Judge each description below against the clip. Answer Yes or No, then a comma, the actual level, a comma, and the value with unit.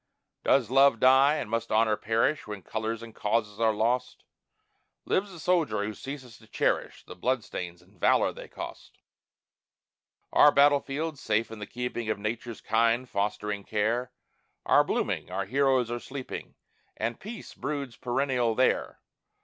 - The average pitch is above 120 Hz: No, low, 115 Hz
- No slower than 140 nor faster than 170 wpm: Yes, average, 155 wpm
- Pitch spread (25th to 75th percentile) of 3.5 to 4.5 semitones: Yes, average, 3.8 semitones